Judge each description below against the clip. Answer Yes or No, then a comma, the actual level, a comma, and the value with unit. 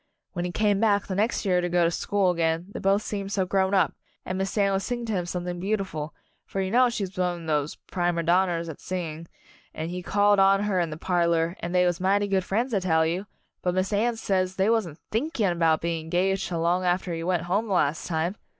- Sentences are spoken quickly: Yes, fast, 240 wpm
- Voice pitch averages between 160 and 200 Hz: Yes, medium, 185 Hz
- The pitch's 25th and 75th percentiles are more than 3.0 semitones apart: No, average, 2.7 semitones